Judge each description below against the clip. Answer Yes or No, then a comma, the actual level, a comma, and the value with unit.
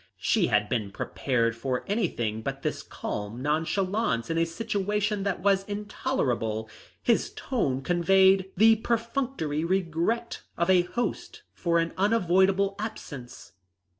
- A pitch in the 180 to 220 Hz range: Yes, medium, 185 Hz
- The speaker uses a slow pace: Yes, slow, 125 wpm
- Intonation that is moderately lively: No, wide, 7.4 semitones